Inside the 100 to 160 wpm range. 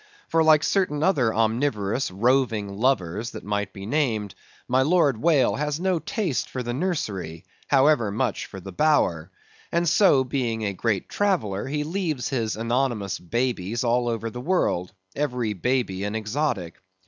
Yes: average, 155 wpm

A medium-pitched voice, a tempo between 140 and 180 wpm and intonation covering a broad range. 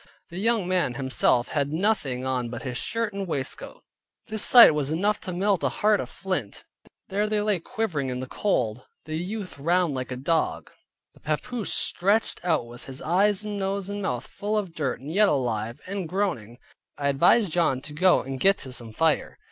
No: medium, 170 Hz; average, 195 wpm; wide, 7.4 semitones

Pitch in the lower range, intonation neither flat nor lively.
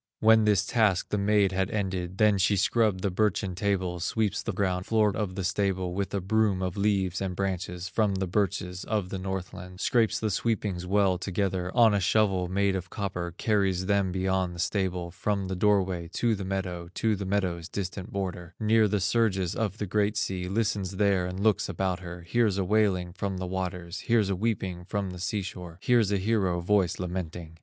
No: very low, 95 Hz; narrow, 2.2 semitones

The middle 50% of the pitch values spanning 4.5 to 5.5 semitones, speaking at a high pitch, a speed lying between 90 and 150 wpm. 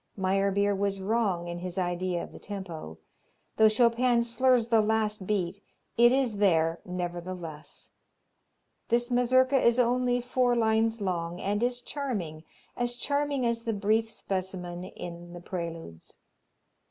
Yes: average, 5.1 semitones; high, 205 Hz; slow, 135 wpm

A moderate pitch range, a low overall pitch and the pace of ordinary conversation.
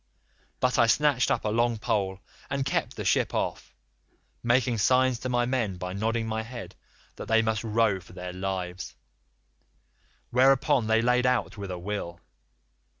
Yes: average, 4.1 semitones; low, 115 Hz; average, 160 wpm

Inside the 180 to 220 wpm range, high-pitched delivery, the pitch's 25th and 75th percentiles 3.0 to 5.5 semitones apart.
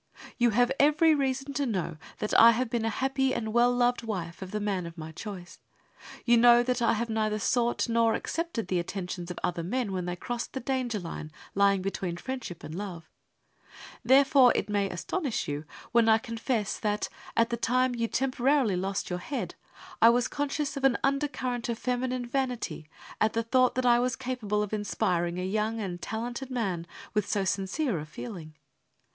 Yes: average, 190 wpm; high, 230 Hz; average, 4.7 semitones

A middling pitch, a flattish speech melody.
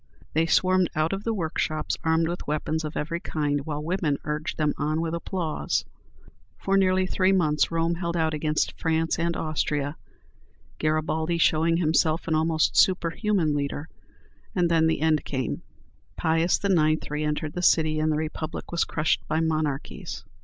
Yes: medium, 160 Hz; narrow, 1.7 semitones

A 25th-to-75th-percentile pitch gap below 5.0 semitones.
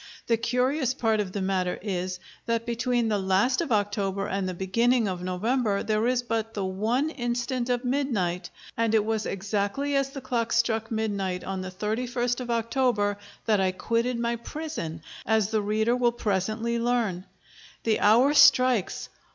Yes: average, 3.6 semitones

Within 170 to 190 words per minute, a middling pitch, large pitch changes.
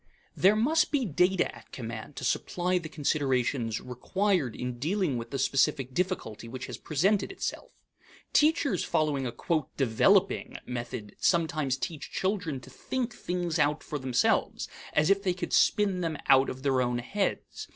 No: average, 155 wpm; medium, 155 Hz; wide, 6.5 semitones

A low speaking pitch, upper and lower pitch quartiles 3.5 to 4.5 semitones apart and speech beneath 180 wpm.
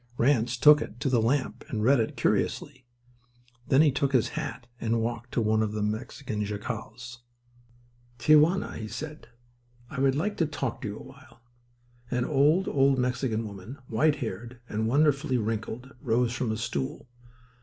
Yes: low, 125 Hz; average, 3.8 semitones; average, 170 wpm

